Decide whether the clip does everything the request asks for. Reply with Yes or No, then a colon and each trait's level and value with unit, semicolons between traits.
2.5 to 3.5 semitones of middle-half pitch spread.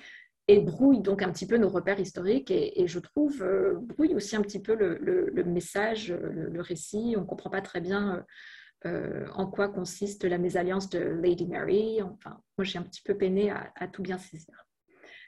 No: average, 4.3 semitones